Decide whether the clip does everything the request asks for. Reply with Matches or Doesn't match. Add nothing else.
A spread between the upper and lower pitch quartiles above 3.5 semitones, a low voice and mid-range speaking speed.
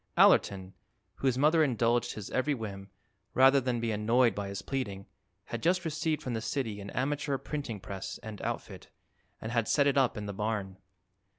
Matches